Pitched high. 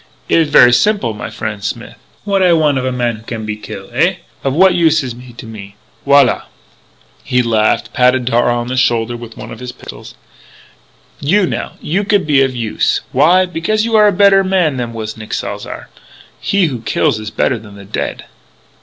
No: low, 125 Hz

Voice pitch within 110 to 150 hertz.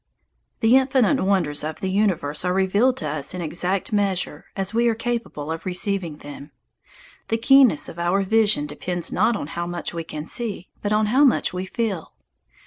No: high, 190 Hz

